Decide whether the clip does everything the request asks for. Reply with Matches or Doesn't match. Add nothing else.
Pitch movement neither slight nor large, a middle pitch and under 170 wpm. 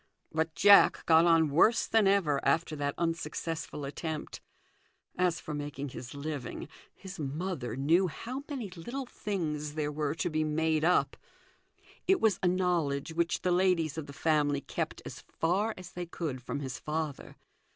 Matches